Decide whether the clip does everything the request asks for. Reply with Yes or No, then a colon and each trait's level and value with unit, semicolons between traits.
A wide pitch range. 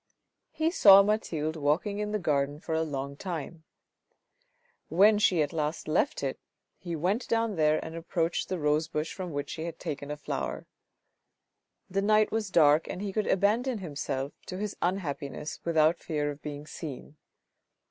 No: average, 4.9 semitones